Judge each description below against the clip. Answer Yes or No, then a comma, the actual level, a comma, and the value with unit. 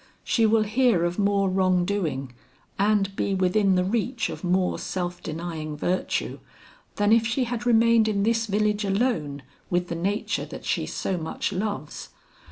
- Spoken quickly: No, average, 165 wpm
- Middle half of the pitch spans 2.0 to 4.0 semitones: Yes, average, 3.6 semitones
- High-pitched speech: Yes, high, 200 Hz